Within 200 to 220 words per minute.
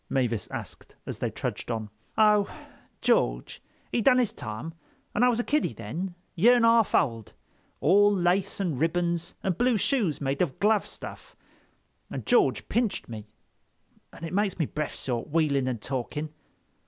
No: average, 165 wpm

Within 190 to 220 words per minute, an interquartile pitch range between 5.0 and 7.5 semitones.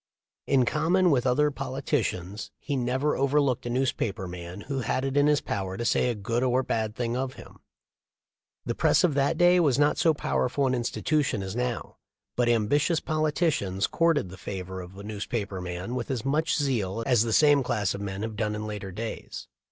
Yes: average, 195 wpm; wide, 5.6 semitones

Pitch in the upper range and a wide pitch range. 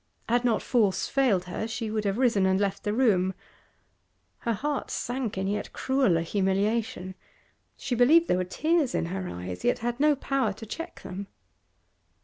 No: high, 215 Hz; average, 5.0 semitones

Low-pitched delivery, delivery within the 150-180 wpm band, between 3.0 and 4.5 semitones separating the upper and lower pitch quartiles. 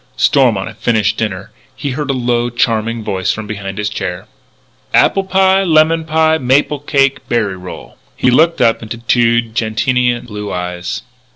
No: low, 120 Hz; average, 160 wpm; average, 4.9 semitones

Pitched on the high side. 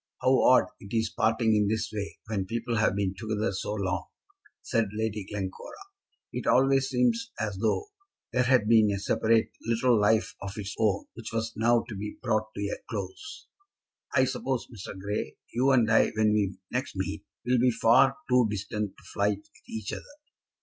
No: low, 110 Hz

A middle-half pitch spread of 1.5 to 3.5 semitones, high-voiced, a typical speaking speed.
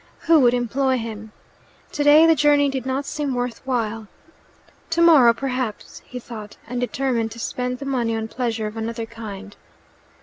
Yes: average, 3.2 semitones; high, 245 Hz; average, 160 wpm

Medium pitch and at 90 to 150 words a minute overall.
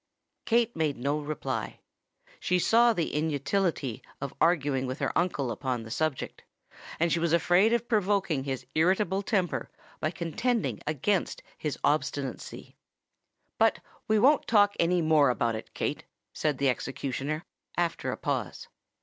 Yes: medium, 160 Hz; average, 140 wpm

